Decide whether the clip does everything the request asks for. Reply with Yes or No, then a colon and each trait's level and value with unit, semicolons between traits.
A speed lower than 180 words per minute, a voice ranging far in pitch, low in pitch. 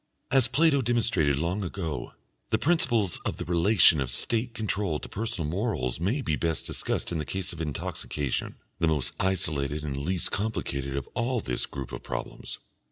Yes: average, 170 wpm; wide, 6.9 semitones; very low, 85 Hz